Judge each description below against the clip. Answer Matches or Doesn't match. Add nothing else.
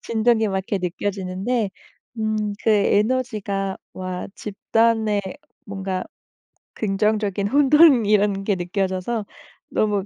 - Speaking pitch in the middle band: Doesn't match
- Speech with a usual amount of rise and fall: Doesn't match